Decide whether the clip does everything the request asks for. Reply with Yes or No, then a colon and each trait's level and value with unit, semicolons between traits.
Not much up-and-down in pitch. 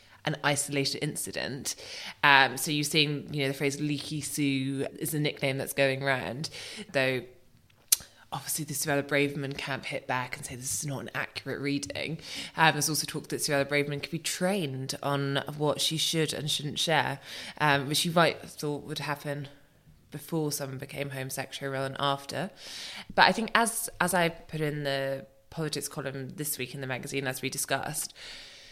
Yes: narrow, 1.8 semitones